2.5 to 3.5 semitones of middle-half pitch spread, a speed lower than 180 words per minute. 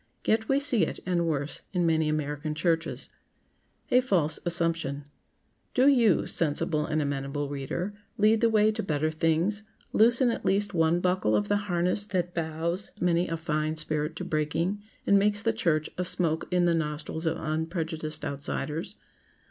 No: average, 4.2 semitones; average, 160 wpm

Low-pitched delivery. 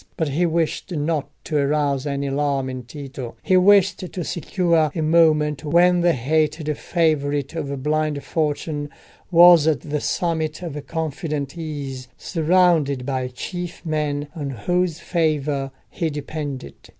No: medium, 150 Hz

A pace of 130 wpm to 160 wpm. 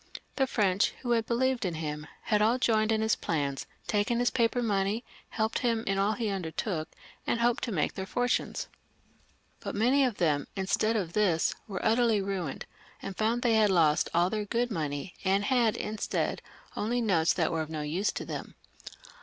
No: average, 185 wpm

